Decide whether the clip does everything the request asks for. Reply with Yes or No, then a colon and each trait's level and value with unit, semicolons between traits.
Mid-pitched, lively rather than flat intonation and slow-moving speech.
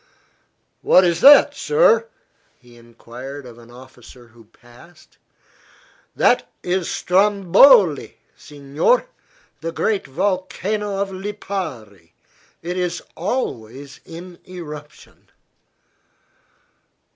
Yes: medium, 170 Hz; wide, 7.5 semitones; slow, 85 wpm